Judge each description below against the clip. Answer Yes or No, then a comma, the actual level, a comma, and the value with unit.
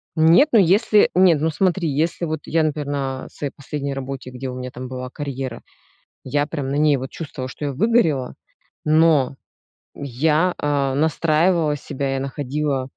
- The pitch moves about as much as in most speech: Yes, average, 3.2 semitones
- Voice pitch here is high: No, medium, 145 Hz